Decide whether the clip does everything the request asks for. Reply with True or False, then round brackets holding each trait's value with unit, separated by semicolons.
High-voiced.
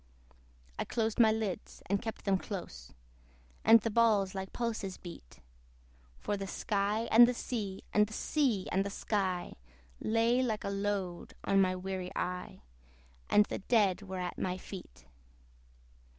True (200 Hz)